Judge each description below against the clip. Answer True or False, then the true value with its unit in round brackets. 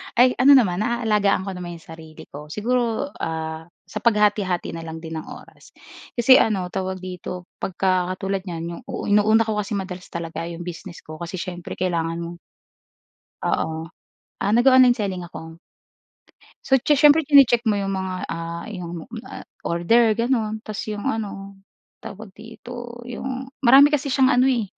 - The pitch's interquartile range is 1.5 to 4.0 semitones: False (5.4 semitones)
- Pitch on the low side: False (195 Hz)